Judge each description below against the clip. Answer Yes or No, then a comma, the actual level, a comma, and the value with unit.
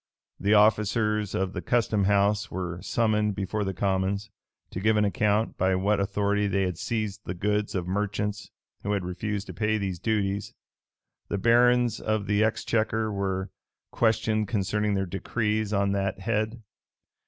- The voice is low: Yes, low, 105 Hz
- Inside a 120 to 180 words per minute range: Yes, average, 155 wpm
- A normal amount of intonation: No, narrow, 1.8 semitones